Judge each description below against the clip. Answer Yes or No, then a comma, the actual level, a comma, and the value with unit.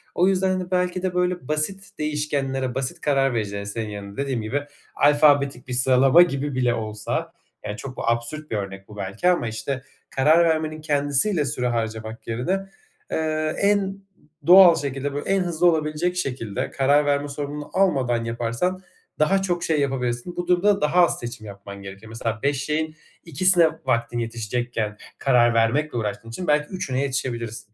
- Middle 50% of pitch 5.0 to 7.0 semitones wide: Yes, wide, 5.4 semitones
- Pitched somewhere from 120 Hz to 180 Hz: Yes, medium, 140 Hz